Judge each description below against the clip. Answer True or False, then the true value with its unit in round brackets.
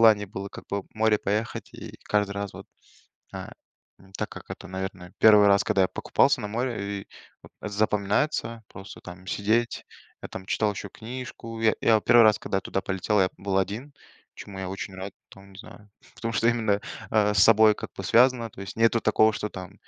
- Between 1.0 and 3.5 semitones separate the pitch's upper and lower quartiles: True (2.4 semitones)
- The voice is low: True (105 Hz)